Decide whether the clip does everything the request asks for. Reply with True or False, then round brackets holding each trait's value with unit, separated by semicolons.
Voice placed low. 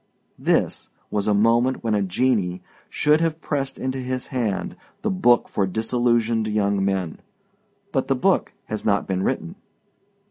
True (115 Hz)